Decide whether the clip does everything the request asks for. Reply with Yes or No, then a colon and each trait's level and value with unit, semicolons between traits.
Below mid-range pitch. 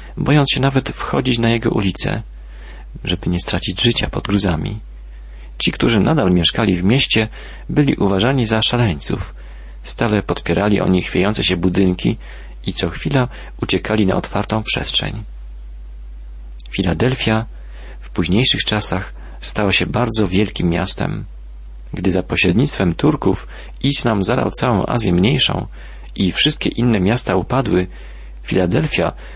Yes: very low, 95 Hz